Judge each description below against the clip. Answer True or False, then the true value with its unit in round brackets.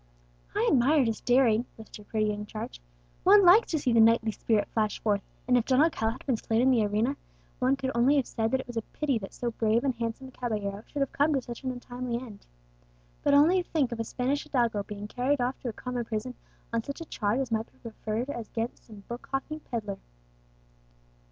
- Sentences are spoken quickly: True (220 wpm)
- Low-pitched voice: False (240 Hz)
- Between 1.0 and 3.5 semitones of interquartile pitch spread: True (3.2 semitones)